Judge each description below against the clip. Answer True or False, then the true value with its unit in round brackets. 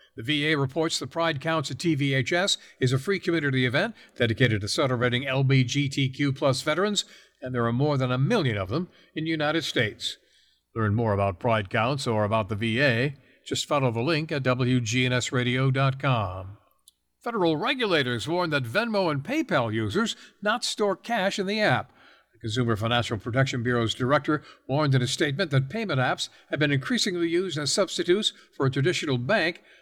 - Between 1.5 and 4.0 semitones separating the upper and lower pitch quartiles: False (5.1 semitones)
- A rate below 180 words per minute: True (165 wpm)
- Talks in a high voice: False (135 Hz)